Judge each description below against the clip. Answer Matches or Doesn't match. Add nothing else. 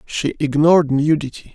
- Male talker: Matches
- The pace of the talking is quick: Doesn't match